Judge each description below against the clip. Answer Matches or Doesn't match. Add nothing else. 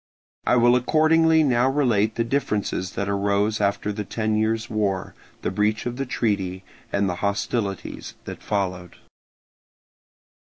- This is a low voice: Matches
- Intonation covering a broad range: Doesn't match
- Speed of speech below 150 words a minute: Matches